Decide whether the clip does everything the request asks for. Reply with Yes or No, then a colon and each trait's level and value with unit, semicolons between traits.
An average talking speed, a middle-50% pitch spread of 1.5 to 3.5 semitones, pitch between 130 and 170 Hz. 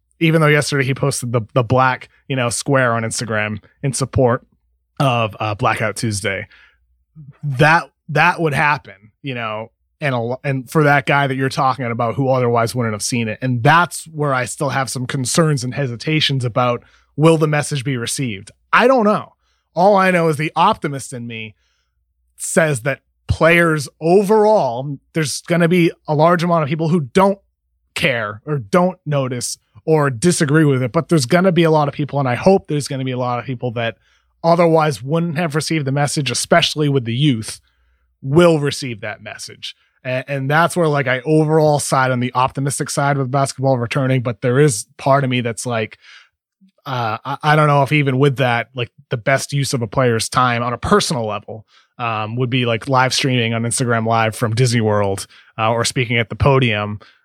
No: average, 195 wpm; average, 4.5 semitones; low, 135 Hz